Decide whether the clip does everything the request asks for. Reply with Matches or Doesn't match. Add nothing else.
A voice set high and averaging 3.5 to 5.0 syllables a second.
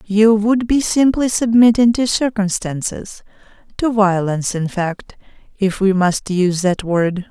Matches